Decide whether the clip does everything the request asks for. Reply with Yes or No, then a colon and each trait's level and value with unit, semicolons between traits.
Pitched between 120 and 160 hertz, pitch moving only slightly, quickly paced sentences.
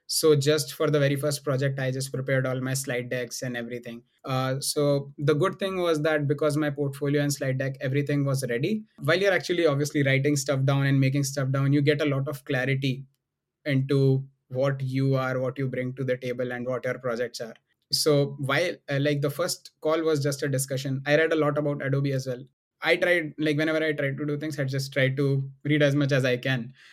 Yes: medium, 140 Hz; narrow, 2.0 semitones; fast, 225 wpm